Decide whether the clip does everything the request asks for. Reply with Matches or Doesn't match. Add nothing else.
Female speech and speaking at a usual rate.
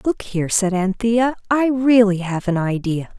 Matches